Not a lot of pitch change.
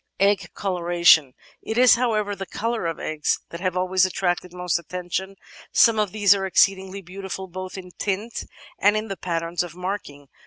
Yes: narrow, 2.3 semitones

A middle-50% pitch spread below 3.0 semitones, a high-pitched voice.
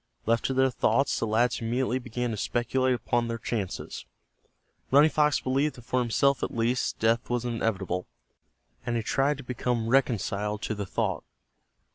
No: narrow, 2.4 semitones; low, 120 Hz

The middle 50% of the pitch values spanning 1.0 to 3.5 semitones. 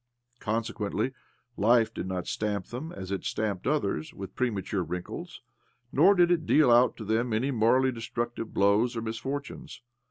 No: average, 4.0 semitones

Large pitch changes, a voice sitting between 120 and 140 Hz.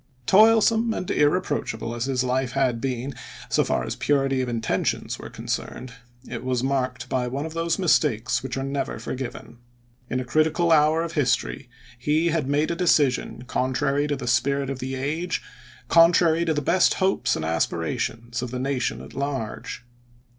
No: average, 4.0 semitones; low, 135 Hz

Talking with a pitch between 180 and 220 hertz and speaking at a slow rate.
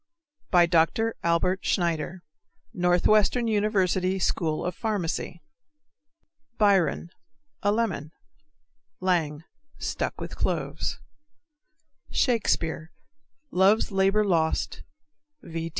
Yes: medium, 185 Hz; slow, 80 wpm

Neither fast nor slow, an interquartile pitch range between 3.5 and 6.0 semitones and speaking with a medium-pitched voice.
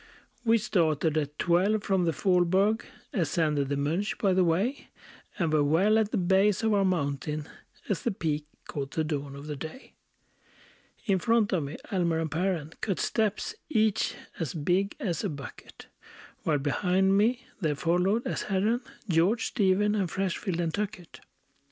Yes: average, 165 wpm; average, 4.6 semitones; medium, 180 Hz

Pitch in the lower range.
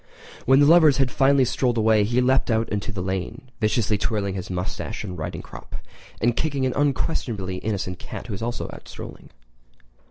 Yes: low, 115 Hz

